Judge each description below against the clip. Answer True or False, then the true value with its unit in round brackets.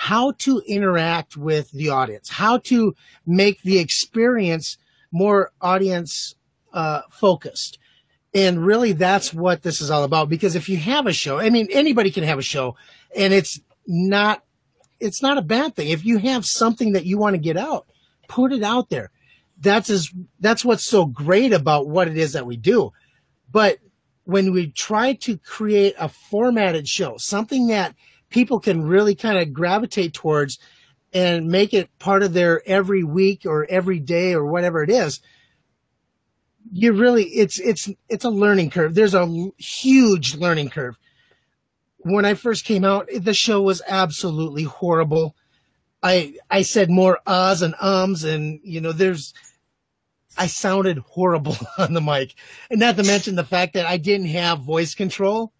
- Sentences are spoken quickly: False (165 wpm)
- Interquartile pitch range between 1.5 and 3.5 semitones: False (3.9 semitones)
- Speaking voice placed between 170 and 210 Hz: True (190 Hz)